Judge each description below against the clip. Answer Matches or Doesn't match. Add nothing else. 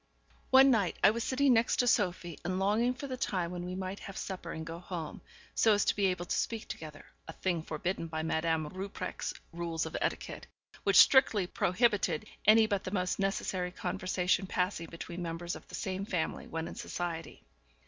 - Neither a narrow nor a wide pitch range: Matches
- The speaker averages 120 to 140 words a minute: Doesn't match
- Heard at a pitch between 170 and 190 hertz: Matches